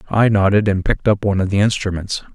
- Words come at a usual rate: No, fast, 230 wpm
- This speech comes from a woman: No, male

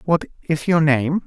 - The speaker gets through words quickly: No, average, 190 wpm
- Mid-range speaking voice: Yes, medium, 155 Hz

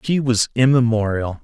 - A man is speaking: Yes, male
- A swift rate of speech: No, slow, 125 wpm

